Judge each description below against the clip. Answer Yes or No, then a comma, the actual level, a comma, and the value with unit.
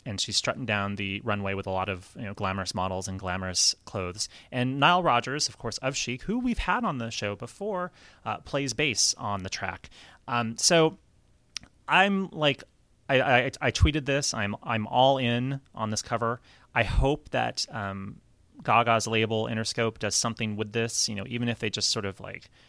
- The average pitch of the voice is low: Yes, low, 115 Hz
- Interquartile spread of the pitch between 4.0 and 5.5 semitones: Yes, average, 4.7 semitones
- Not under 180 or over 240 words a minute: Yes, average, 195 wpm